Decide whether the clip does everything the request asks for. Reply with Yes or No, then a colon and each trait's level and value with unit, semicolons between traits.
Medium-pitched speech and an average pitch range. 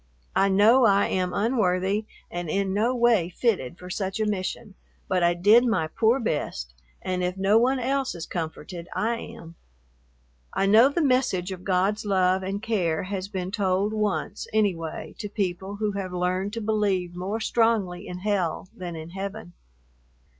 No: high, 195 Hz; average, 3.2 semitones